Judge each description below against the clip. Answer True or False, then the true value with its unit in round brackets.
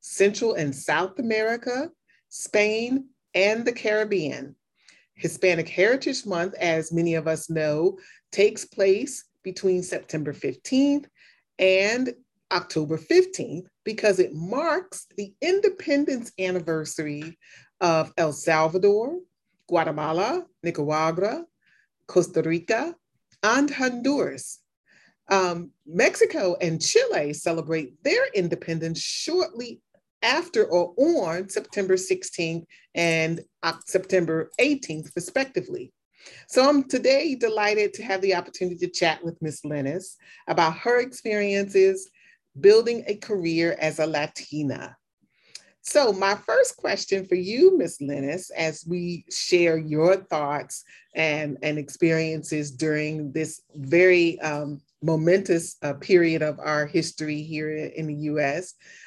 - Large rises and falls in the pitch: True (6.7 semitones)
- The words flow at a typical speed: False (110 wpm)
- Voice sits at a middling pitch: True (180 Hz)